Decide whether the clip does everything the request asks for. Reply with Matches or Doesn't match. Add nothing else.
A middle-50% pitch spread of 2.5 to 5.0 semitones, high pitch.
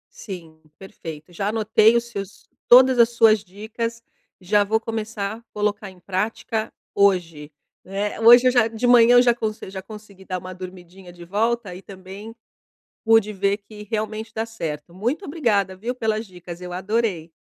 Matches